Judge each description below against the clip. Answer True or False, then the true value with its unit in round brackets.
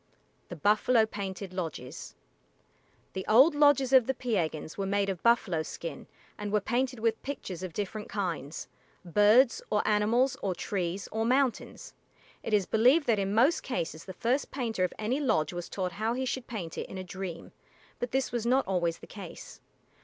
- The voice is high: True (210 Hz)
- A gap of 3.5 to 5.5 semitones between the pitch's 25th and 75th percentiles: True (4.9 semitones)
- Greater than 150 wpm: True (180 wpm)